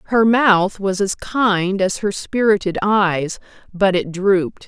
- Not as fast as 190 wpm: Yes, average, 155 wpm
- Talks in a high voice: Yes, high, 195 Hz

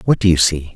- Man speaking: Yes, male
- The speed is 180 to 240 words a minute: No, fast, 315 wpm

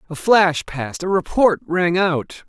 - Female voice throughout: No, male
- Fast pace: No, average, 170 wpm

